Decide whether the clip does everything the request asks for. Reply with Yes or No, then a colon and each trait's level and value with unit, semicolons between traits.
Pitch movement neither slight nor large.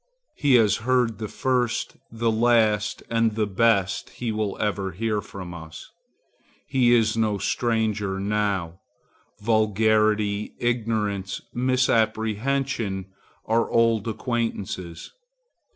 No: narrow, 2.3 semitones